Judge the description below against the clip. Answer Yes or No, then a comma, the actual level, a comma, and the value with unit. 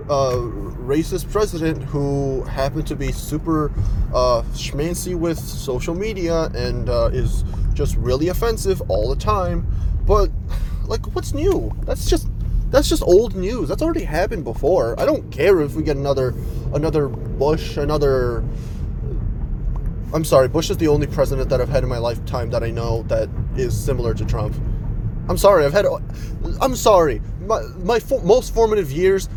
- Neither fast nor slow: Yes, average, 160 wpm